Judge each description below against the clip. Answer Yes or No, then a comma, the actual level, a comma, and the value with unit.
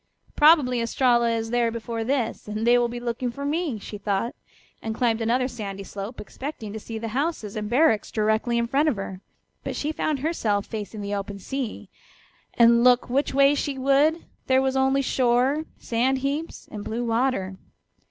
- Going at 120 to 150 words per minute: No, average, 180 wpm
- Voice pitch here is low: No, high, 240 Hz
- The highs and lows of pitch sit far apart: No, average, 3.6 semitones